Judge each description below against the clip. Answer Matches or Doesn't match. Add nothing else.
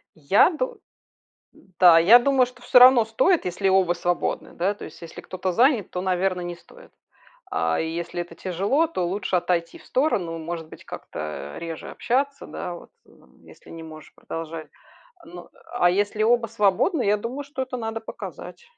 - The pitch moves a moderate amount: Doesn't match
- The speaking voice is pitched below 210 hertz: Matches